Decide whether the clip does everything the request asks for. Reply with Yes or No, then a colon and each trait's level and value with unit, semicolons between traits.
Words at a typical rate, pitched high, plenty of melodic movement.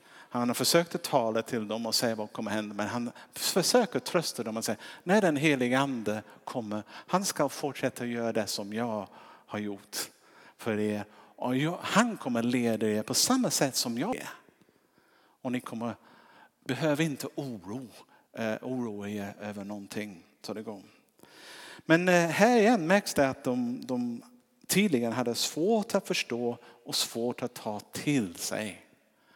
No: average, 170 wpm; low, 125 Hz; wide, 7.3 semitones